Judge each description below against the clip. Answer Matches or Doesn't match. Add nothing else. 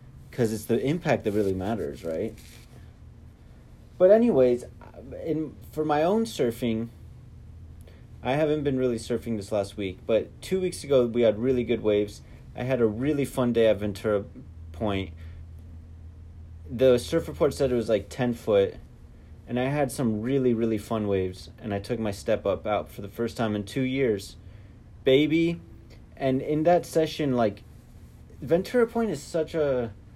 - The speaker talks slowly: Doesn't match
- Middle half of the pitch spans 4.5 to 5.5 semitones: Matches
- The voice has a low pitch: Matches